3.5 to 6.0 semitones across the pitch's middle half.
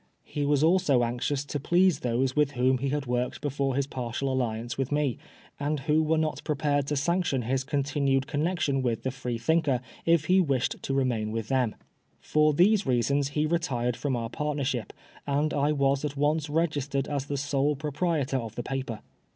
No: narrow, 2.5 semitones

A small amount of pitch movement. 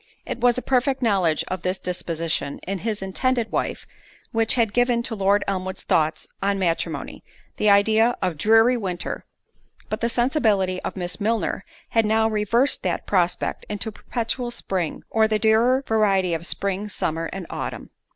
No: average, 3.7 semitones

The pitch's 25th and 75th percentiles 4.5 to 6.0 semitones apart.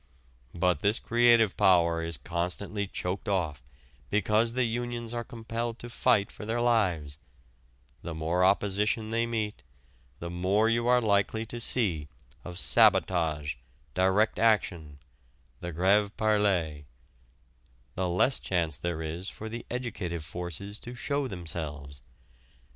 Yes: average, 4.8 semitones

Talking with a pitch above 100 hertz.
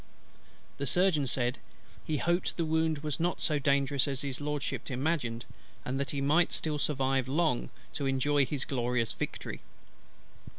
Yes: medium, 140 Hz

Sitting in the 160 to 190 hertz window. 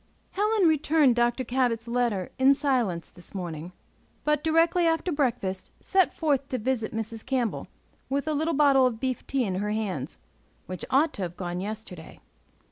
No: very high, 250 Hz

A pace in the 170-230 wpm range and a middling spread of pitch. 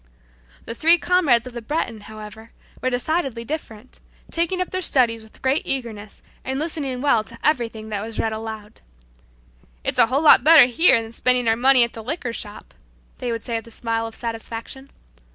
Yes: average, 190 wpm; average, 3.6 semitones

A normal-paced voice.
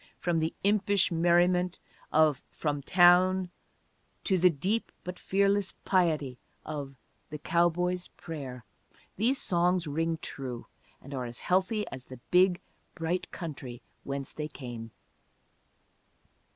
No: slow, 120 wpm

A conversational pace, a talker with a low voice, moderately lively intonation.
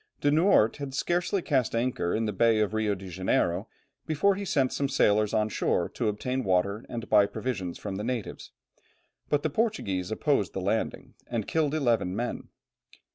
No: average, 175 wpm; low, 115 Hz; wide, 5.7 semitones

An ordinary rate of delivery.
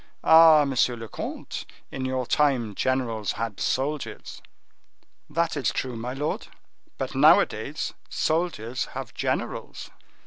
No: slow, 115 wpm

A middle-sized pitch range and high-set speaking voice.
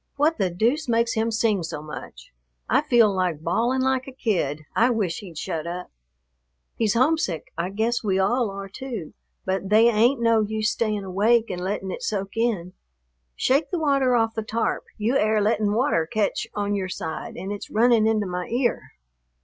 Yes: average, 3.9 semitones; high, 215 Hz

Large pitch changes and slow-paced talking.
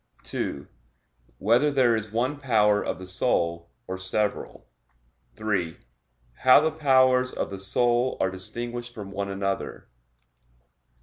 No: average, 4.7 semitones; slow, 125 wpm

